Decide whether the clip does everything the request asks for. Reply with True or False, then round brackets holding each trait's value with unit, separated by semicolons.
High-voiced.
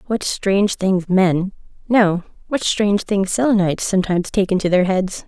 True (195 Hz)